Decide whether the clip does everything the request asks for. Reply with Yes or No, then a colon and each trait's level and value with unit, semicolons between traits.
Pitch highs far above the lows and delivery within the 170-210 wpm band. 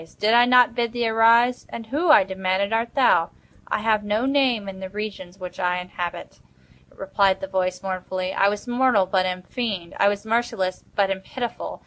No: average, 3.9 semitones; average, 190 wpm